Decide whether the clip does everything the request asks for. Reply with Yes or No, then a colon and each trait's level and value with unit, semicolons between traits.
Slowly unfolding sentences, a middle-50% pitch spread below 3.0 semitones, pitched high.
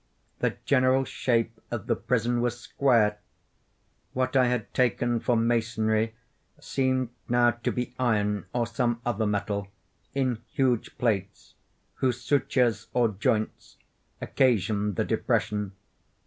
No: slow, 120 wpm; narrow, 2.4 semitones; low, 120 Hz